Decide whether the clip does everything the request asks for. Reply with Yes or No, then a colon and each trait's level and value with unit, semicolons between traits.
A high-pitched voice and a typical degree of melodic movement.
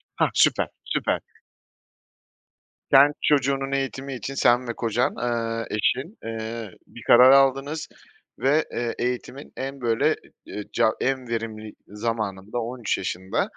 No: low, 120 Hz; average, 3.1 semitones